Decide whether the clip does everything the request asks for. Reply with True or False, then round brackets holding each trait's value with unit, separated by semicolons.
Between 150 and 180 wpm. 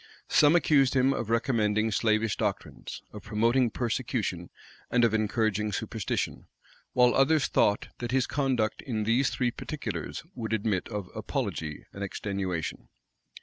False (135 wpm)